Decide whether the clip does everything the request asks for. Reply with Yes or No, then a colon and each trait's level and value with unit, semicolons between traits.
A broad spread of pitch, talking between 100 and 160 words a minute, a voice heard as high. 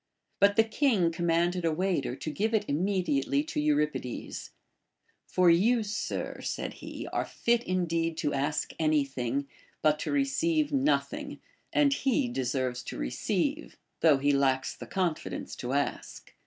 No: wide, 7.1 semitones; average, 155 wpm; medium, 165 Hz